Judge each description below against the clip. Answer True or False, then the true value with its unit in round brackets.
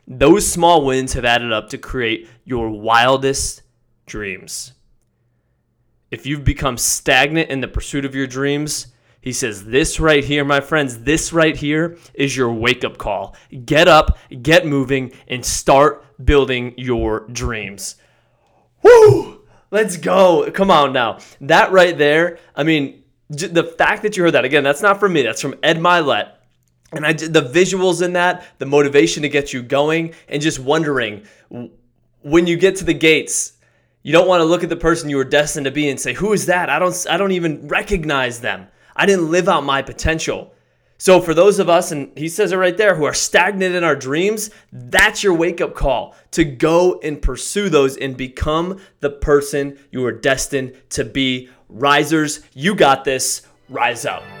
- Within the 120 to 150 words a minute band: False (180 wpm)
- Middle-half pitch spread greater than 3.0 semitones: True (4.5 semitones)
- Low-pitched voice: False (145 Hz)